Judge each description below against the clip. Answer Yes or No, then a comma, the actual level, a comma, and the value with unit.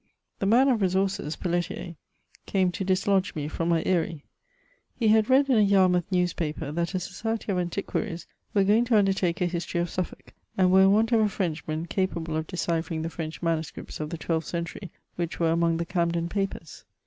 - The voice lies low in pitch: No, medium, 180 Hz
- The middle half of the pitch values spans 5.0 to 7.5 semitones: No, average, 2.8 semitones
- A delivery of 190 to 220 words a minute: Yes, average, 195 wpm